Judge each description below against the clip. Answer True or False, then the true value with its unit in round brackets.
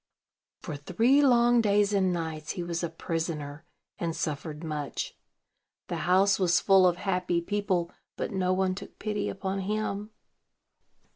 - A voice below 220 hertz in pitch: True (185 Hz)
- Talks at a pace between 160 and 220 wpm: False (145 wpm)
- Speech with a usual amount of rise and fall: True (3.4 semitones)